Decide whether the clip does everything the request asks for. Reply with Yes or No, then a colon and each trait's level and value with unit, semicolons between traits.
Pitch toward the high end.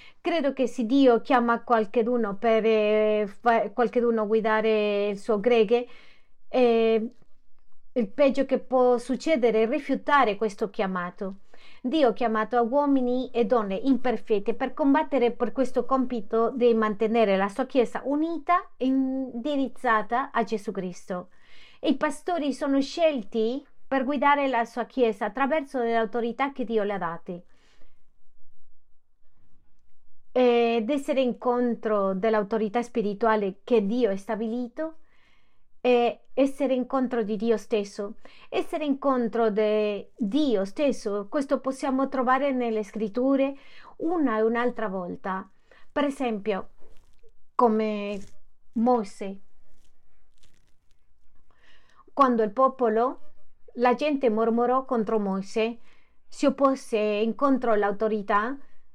Yes: high, 240 Hz